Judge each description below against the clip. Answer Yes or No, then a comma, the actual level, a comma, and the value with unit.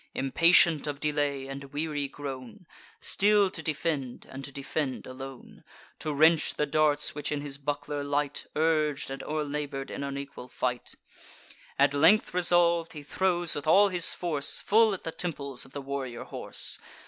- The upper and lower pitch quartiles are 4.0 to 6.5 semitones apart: No, average, 2.9 semitones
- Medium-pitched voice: Yes, medium, 145 Hz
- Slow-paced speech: No, average, 160 wpm